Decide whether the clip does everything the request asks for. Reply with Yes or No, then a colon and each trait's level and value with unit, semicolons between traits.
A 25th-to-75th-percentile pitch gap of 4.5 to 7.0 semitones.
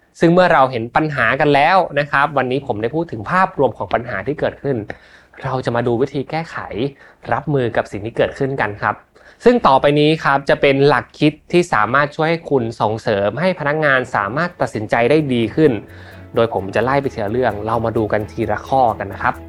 Yes: average, 4.9 semitones